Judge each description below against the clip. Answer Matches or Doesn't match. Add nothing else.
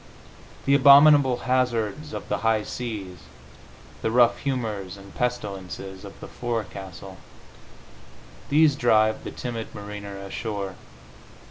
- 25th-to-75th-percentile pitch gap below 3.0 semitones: Doesn't match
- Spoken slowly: Matches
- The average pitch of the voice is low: Matches